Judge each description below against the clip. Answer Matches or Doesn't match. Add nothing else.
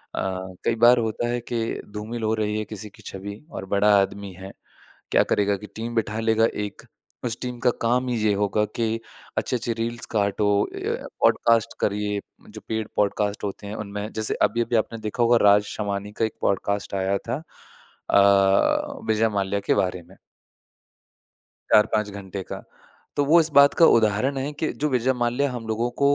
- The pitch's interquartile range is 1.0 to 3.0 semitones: Matches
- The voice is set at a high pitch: Doesn't match